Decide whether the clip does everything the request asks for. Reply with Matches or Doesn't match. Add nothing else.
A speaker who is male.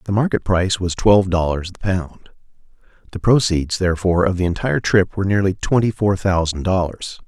Matches